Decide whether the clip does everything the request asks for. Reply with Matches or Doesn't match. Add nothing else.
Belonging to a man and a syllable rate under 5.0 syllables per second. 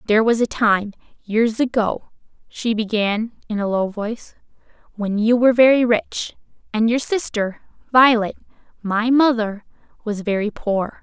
Doesn't match